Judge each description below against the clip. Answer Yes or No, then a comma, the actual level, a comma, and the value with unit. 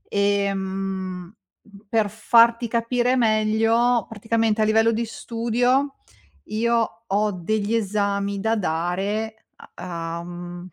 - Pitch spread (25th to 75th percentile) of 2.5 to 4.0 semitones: Yes, average, 2.9 semitones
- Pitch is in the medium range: No, high, 215 Hz